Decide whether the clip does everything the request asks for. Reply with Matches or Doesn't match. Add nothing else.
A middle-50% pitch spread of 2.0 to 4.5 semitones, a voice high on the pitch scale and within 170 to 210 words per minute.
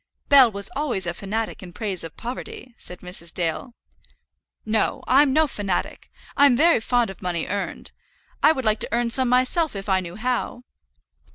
Doesn't match